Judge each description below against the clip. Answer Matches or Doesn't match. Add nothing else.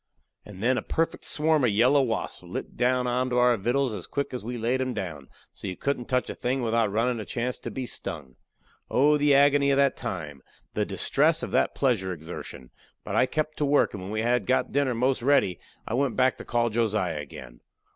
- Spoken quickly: Matches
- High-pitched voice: Doesn't match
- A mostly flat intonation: Doesn't match